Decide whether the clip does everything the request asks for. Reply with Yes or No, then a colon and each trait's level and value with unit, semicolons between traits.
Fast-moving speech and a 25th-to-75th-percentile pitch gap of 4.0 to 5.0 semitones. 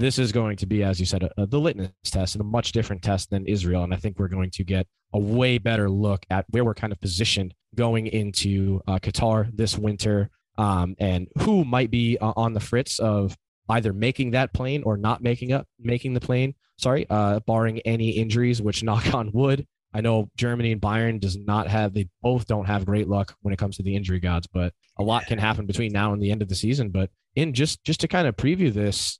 No: fast, 240 wpm; average, 3.2 semitones